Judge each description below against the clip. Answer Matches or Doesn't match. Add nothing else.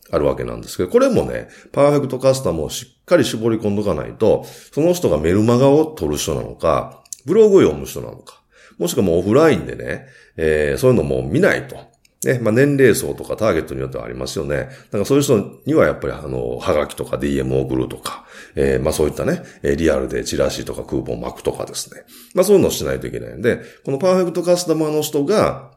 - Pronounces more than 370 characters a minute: Matches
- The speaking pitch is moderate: Doesn't match